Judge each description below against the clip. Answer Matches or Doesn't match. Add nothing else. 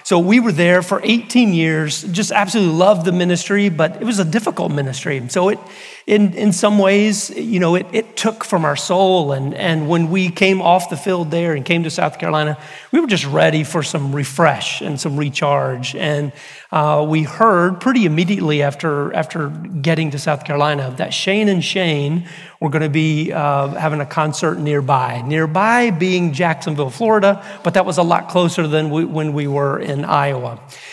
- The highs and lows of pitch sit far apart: Doesn't match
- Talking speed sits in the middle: Matches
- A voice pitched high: Doesn't match